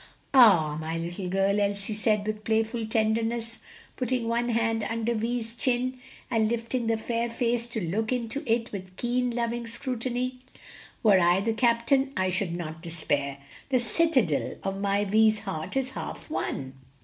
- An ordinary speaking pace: Yes, average, 160 wpm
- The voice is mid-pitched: No, high, 225 Hz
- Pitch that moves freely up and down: No, average, 3.3 semitones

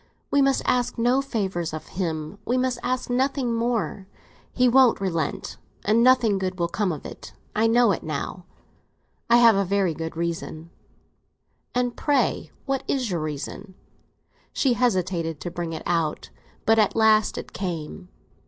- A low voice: No, high, 205 Hz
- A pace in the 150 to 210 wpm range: Yes, average, 155 wpm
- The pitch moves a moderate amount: No, wide, 6.2 semitones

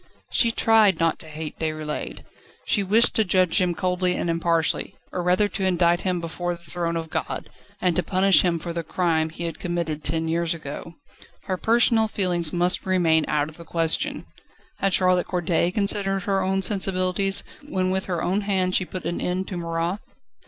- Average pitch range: No, narrow, 2.2 semitones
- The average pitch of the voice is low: No, medium, 180 Hz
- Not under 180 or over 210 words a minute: Yes, average, 190 wpm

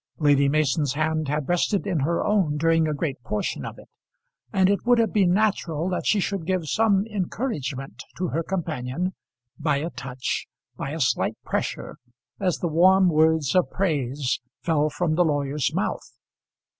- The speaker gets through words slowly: No, average, 170 wpm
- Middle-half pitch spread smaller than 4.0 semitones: No, average, 4.3 semitones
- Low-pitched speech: No, medium, 160 Hz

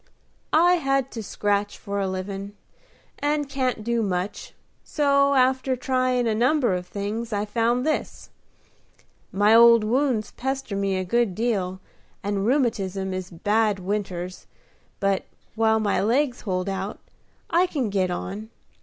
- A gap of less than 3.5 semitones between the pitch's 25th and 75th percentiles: No, average, 4.5 semitones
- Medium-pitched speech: No, high, 215 Hz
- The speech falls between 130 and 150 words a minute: Yes, average, 140 wpm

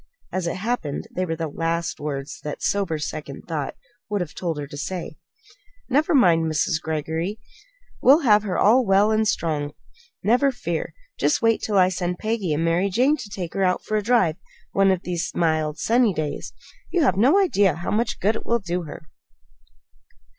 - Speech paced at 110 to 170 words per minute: No, average, 190 wpm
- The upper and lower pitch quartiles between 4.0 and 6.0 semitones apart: Yes, average, 5.2 semitones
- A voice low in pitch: No, medium, 185 Hz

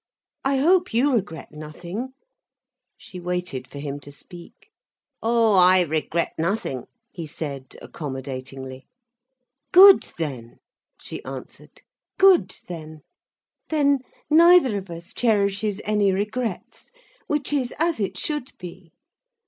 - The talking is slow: Yes, slow, 115 wpm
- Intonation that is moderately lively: No, wide, 8.5 semitones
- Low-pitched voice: No, high, 190 Hz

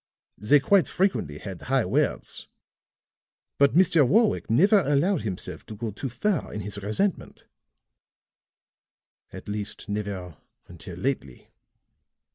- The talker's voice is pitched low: Yes, low, 115 Hz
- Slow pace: Yes, slow, 115 wpm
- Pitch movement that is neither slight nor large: No, wide, 8.9 semitones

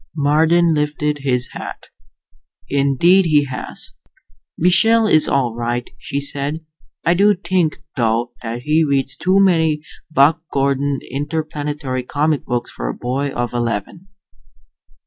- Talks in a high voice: No, medium, 145 Hz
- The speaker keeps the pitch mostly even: No, average, 3.7 semitones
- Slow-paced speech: Yes, slow, 125 wpm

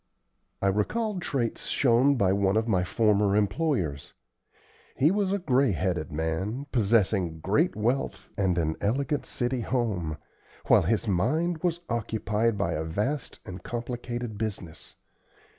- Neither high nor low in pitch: No, low, 110 Hz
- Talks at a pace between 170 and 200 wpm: No, slow, 135 wpm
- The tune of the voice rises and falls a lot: Yes, wide, 5.8 semitones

